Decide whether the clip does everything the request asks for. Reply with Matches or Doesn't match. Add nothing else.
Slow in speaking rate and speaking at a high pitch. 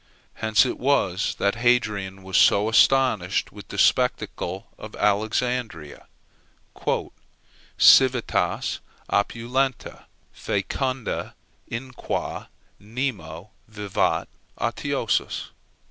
Doesn't match